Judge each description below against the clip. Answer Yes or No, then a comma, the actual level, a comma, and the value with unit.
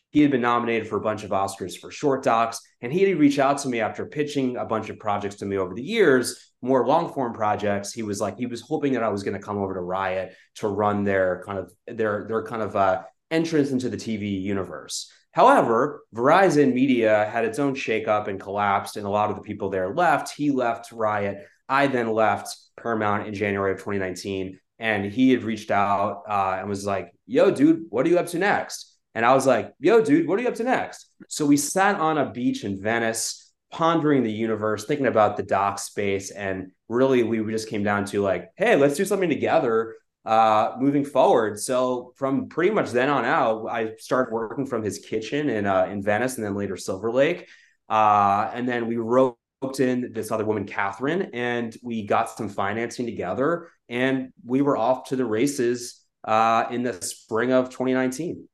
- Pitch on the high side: No, low, 115 Hz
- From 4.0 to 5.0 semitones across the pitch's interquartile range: Yes, average, 4.3 semitones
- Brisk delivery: Yes, fast, 210 wpm